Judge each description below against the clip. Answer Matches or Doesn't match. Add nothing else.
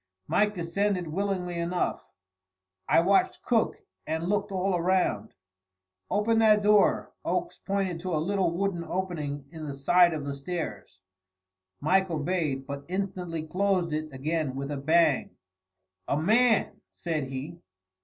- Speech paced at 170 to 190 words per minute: Doesn't match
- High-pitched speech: Doesn't match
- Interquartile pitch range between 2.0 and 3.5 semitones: Doesn't match